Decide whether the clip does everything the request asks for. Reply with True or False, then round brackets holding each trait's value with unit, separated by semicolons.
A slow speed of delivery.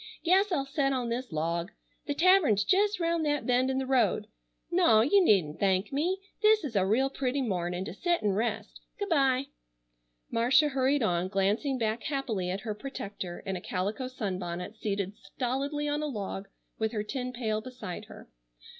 False (180 wpm)